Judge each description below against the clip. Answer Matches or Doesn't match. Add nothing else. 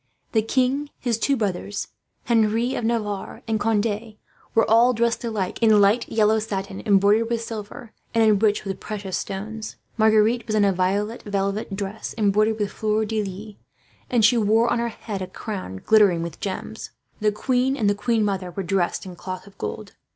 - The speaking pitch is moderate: Doesn't match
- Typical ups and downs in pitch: Doesn't match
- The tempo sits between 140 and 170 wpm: Doesn't match